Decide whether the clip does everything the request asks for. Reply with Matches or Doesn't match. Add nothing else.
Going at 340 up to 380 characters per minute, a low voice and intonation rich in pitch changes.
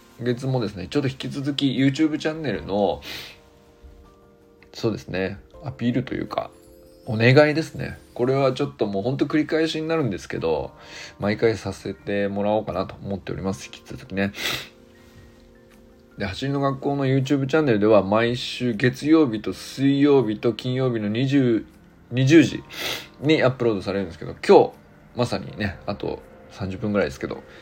Matches